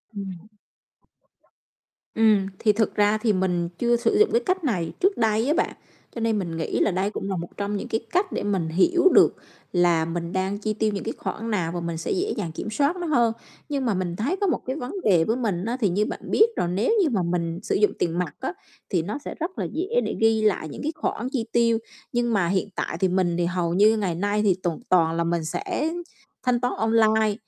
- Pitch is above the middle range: Yes, high, 210 Hz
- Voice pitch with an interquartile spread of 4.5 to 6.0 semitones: Yes, average, 5.2 semitones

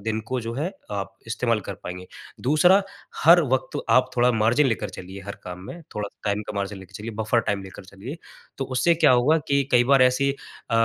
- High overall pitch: No, low, 115 Hz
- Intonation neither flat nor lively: Yes, average, 4.8 semitones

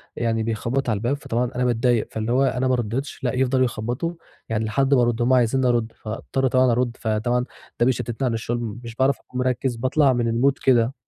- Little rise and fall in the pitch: Yes, narrow, 2.0 semitones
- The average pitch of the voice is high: No, low, 120 Hz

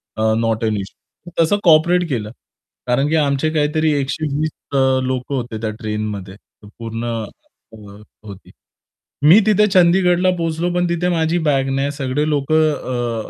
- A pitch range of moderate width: No, wide, 6.1 semitones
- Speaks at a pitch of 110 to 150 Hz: Yes, medium, 140 Hz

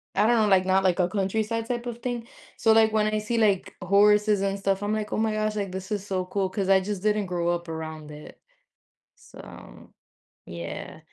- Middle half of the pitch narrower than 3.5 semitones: Yes, narrow, 2.4 semitones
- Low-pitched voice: No, high, 200 Hz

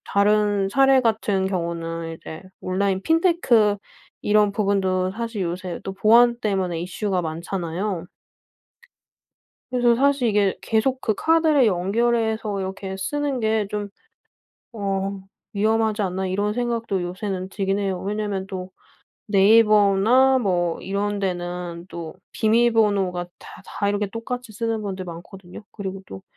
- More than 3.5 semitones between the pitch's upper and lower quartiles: No, average, 3.0 semitones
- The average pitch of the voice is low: No, high, 200 Hz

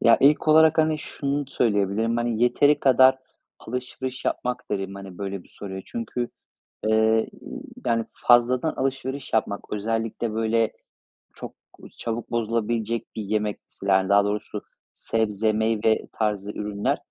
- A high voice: No, low, 115 Hz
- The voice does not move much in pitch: No, average, 3.2 semitones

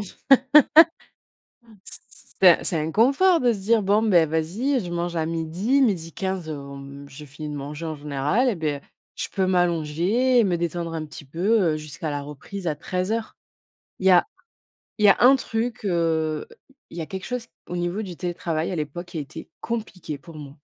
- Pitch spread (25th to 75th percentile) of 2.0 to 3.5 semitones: No, average, 4.8 semitones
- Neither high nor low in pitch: Yes, medium, 175 Hz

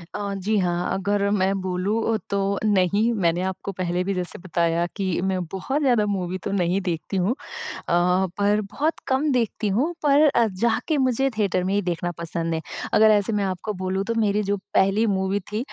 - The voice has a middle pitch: No, high, 200 Hz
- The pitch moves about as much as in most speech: Yes, average, 3.0 semitones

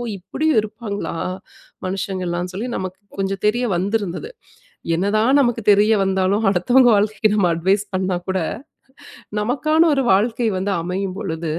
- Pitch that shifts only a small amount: No, average, 3.3 semitones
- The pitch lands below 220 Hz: Yes, high, 200 Hz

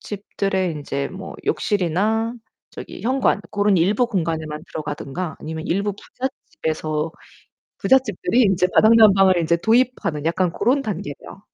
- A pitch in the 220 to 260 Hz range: No, high, 190 Hz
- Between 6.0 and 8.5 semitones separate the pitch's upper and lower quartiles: No, average, 5.2 semitones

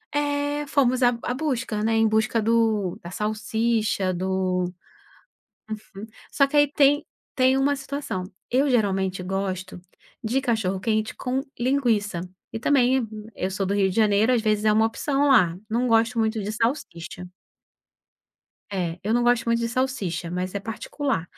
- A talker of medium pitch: No, high, 225 Hz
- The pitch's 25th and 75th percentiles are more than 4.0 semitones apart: Yes, average, 4.9 semitones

